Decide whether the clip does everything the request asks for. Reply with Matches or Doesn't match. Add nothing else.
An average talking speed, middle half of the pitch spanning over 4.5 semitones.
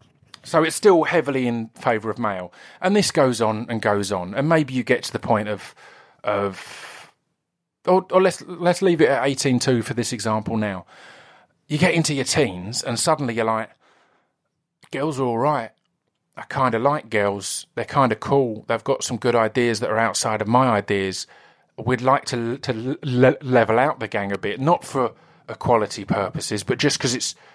Doesn't match